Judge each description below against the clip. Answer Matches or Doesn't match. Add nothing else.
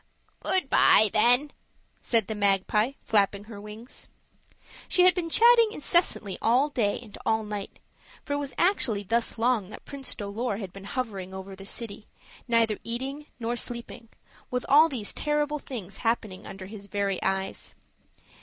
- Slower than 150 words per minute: Doesn't match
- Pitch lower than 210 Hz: Doesn't match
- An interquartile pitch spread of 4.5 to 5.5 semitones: Matches